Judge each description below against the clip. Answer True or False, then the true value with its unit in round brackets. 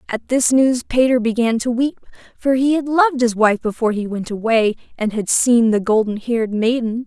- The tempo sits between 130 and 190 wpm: False (205 wpm)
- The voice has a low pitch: False (235 Hz)